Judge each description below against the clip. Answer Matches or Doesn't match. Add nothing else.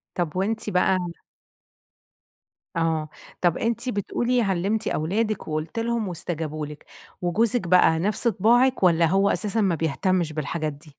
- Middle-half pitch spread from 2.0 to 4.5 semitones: Doesn't match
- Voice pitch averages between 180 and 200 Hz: Matches